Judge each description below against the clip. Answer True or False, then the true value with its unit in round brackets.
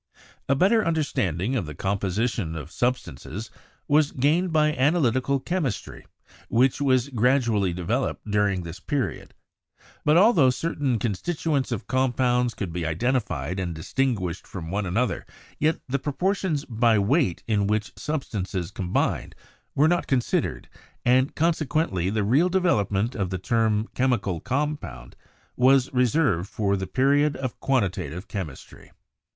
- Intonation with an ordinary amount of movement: False (6.4 semitones)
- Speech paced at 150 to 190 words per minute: False (140 wpm)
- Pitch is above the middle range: False (120 Hz)